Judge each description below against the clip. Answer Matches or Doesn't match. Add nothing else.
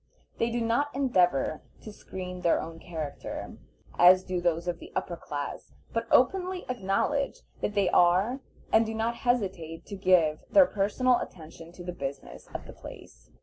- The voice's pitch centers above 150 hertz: Matches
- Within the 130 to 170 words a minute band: Matches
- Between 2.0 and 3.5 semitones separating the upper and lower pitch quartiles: Doesn't match